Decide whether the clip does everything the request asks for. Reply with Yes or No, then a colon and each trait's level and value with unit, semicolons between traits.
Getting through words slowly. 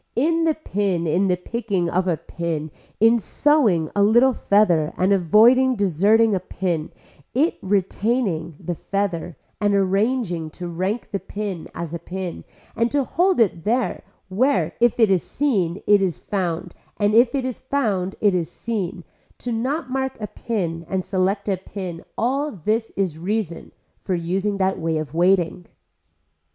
No: average, 165 wpm